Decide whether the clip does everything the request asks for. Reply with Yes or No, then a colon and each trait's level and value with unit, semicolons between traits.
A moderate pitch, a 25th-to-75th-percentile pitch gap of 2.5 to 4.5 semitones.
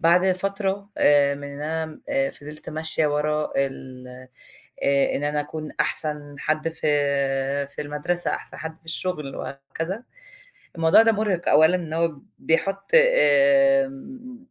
No: medium, 160 Hz; average, 4.9 semitones